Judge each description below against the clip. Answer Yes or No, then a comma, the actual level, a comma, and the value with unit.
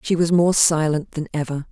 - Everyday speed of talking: No, fast, 210 wpm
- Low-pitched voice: No, medium, 160 Hz